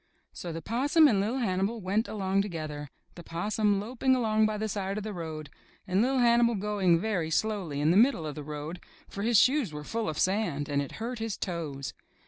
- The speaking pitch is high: Yes, high, 200 Hz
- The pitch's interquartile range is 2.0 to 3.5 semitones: No, average, 5.2 semitones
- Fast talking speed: Yes, fast, 215 wpm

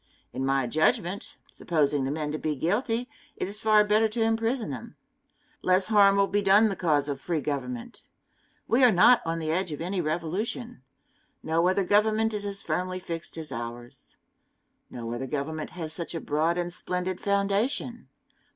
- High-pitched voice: No, medium, 180 Hz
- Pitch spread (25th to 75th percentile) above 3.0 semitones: Yes, average, 5.2 semitones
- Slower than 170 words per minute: No, average, 175 wpm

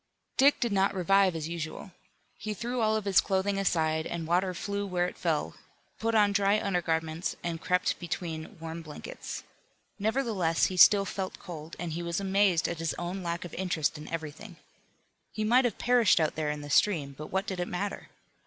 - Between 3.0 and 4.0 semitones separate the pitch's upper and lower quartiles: Yes, average, 3.6 semitones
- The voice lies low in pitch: No, medium, 180 Hz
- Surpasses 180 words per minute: Yes, average, 190 wpm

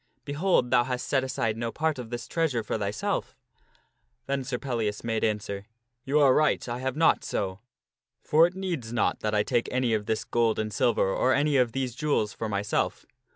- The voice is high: No, low, 120 Hz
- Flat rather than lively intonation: No, average, 3.9 semitones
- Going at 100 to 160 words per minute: No, average, 200 wpm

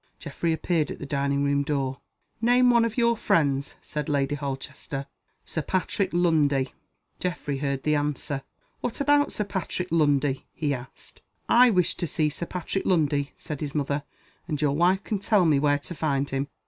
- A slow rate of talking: No, average, 175 wpm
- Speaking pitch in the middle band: Yes, medium, 150 Hz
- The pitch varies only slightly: No, average, 4.3 semitones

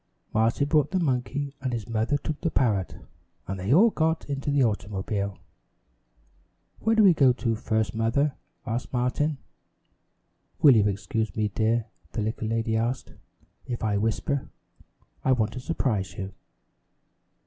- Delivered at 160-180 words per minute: No, average, 145 wpm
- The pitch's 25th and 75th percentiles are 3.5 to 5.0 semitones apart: Yes, average, 4.5 semitones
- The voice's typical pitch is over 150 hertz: No, low, 120 Hz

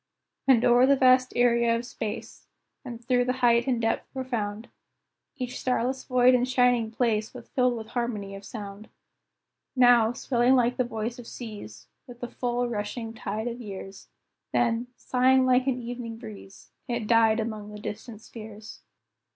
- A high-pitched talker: Yes, high, 235 Hz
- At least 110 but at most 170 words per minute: Yes, average, 160 wpm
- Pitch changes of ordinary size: No, narrow, 2.2 semitones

